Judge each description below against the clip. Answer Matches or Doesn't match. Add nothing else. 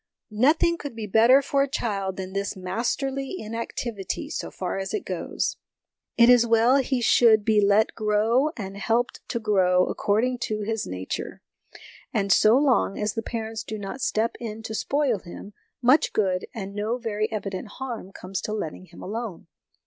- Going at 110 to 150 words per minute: Doesn't match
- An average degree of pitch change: Matches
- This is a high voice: Matches